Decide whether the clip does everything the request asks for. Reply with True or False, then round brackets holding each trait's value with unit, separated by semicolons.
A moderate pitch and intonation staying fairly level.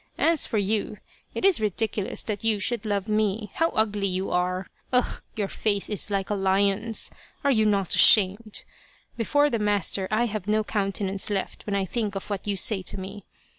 False (205 Hz; 2.0 semitones)